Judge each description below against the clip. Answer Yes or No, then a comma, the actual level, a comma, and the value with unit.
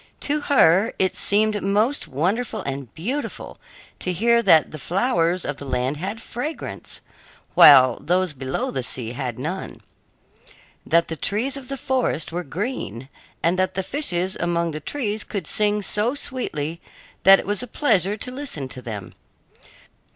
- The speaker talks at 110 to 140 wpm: No, average, 160 wpm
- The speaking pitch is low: No, medium, 185 Hz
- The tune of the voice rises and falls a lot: Yes, wide, 7.0 semitones